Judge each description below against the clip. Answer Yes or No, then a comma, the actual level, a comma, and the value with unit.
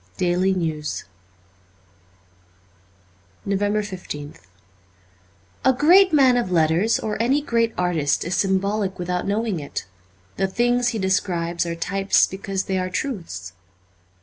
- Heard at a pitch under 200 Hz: Yes, high, 190 Hz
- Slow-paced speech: Yes, slow, 125 wpm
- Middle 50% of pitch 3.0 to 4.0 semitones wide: No, average, 4.4 semitones